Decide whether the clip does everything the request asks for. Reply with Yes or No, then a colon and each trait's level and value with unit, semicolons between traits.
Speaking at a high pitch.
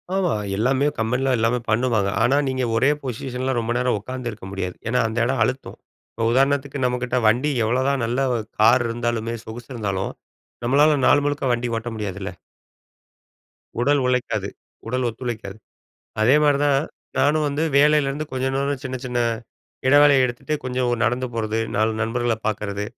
No: low, 125 Hz